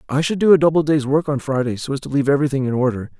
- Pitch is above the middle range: No, medium, 140 Hz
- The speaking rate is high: Yes, fast, 300 wpm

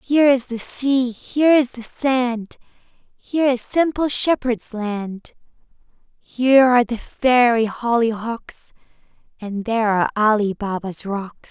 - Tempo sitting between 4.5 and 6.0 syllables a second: No, 4.1 syllables/s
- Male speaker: No, female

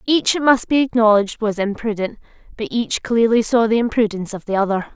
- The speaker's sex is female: Yes, female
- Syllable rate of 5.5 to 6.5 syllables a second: Yes, 5.9 syllables/s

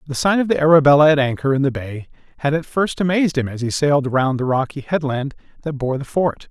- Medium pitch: Yes, medium, 145 Hz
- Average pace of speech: No, fast, 240 wpm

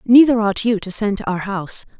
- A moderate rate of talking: No, fast, 240 wpm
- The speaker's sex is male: No, female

